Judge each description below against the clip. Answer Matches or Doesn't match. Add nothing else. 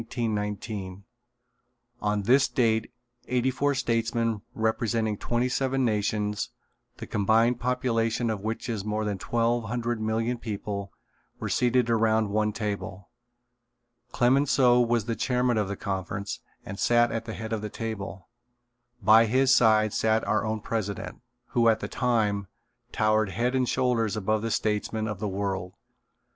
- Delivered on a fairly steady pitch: Matches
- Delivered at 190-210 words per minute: Doesn't match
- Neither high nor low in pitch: Doesn't match